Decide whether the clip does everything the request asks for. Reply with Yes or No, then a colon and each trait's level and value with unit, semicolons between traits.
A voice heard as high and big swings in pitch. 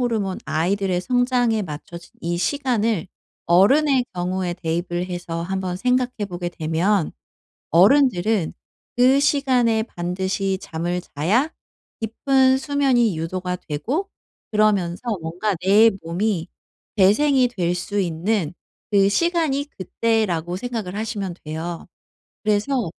Yes: high, 195 Hz; wide, 5.8 semitones